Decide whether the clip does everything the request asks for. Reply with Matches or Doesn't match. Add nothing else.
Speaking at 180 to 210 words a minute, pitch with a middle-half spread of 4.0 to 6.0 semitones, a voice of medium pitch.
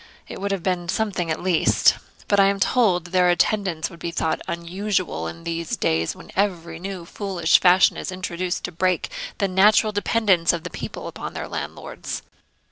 Doesn't match